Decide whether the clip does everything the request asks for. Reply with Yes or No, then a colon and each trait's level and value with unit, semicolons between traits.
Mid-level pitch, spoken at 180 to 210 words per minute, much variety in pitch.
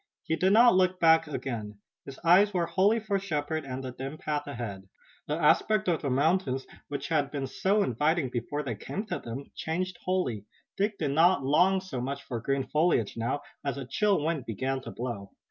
Yes: medium, 150 Hz; average, 195 wpm; wide, 5.7 semitones